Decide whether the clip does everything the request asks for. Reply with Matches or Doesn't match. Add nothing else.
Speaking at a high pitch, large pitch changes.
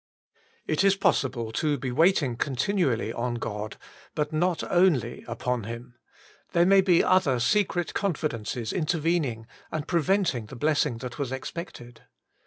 Doesn't match